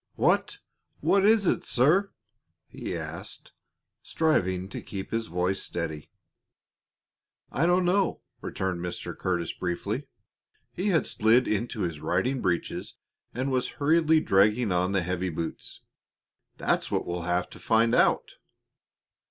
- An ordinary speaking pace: No, slow, 130 wpm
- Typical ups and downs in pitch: No, wide, 8.6 semitones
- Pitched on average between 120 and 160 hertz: No, low, 105 Hz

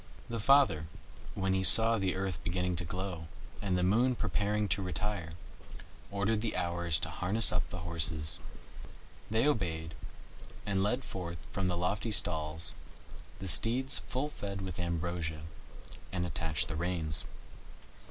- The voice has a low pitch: Yes, very low, 90 Hz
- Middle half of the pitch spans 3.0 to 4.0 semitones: Yes, average, 3.7 semitones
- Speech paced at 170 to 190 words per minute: No, average, 140 wpm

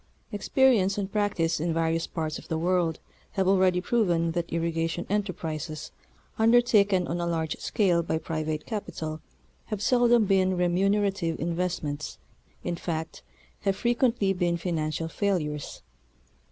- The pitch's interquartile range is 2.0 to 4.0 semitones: Yes, average, 3.5 semitones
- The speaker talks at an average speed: No, slow, 130 wpm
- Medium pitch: Yes, medium, 175 Hz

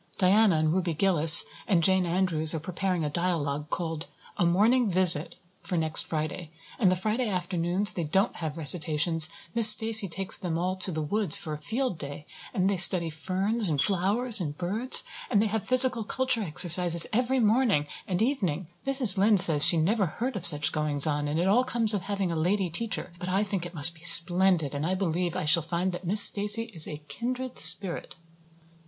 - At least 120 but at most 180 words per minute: No, average, 195 wpm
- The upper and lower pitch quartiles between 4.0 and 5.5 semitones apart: Yes, average, 4.3 semitones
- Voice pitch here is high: No, medium, 180 Hz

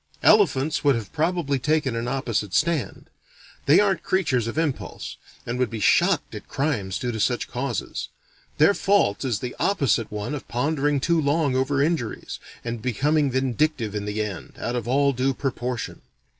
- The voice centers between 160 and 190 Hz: No, low, 130 Hz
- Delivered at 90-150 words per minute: No, average, 170 wpm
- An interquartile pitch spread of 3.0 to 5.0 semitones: Yes, average, 4.2 semitones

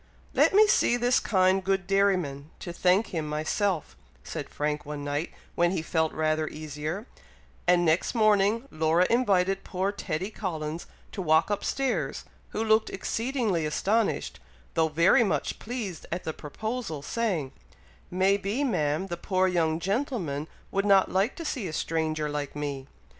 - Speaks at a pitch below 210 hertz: Yes, medium, 185 Hz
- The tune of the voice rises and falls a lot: No, average, 4.7 semitones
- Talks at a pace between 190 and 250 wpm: No, average, 155 wpm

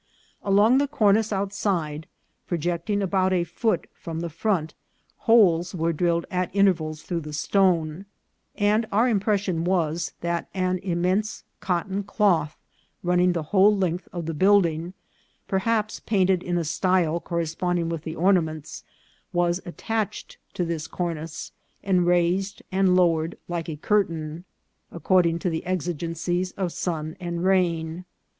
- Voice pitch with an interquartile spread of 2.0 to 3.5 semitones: Yes, average, 2.7 semitones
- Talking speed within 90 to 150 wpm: Yes, average, 140 wpm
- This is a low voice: No, medium, 175 Hz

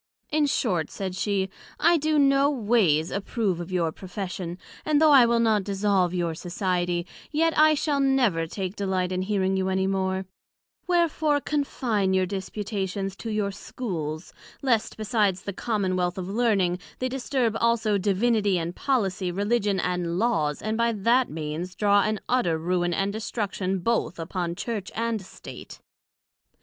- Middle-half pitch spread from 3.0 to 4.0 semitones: No, average, 4.4 semitones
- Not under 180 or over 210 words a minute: No, average, 155 wpm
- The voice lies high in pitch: Yes, high, 200 Hz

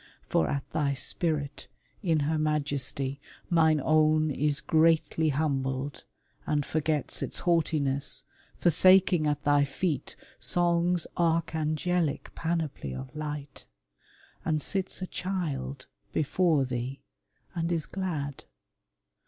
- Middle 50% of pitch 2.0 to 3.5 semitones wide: Yes, average, 2.9 semitones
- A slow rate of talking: Yes, slow, 105 wpm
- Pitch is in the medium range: Yes, medium, 155 Hz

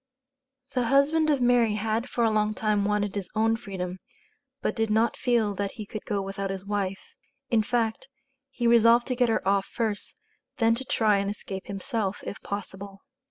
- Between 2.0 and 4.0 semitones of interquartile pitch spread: Yes, average, 2.8 semitones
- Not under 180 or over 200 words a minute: Yes, average, 185 wpm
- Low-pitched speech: No, high, 215 Hz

